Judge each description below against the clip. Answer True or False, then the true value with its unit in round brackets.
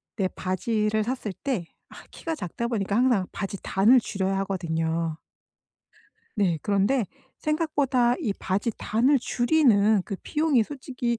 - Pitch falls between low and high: False (220 Hz)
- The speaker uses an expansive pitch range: False (4.7 semitones)